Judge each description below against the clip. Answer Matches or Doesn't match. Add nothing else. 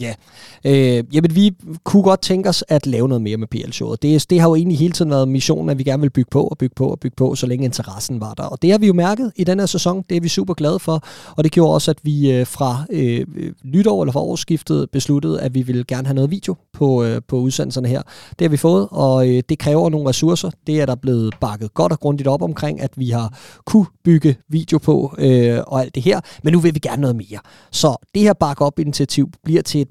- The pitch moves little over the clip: Doesn't match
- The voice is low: Doesn't match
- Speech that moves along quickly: Matches